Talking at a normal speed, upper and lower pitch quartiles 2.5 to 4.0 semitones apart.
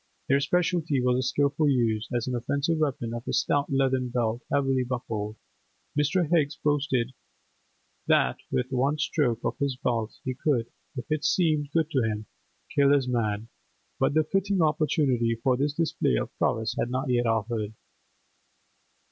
Yes: average, 160 wpm; average, 3.7 semitones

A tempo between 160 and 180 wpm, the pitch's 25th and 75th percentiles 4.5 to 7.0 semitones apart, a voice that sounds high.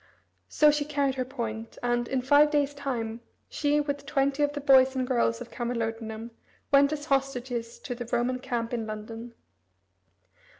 No: average, 165 wpm; average, 3.3 semitones; very high, 255 Hz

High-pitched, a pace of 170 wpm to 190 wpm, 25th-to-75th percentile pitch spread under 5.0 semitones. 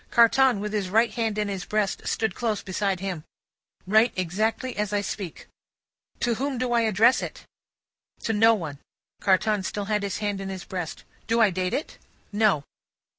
Yes: high, 210 Hz; average, 180 wpm; average, 2.8 semitones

